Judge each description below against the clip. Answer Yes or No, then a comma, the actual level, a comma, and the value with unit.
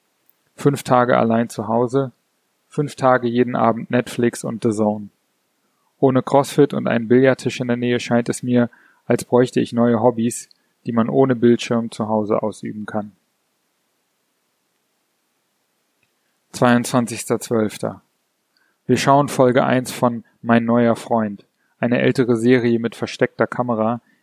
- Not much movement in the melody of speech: Yes, narrow, 1.6 semitones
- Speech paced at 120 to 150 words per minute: Yes, average, 130 wpm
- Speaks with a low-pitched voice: Yes, low, 120 Hz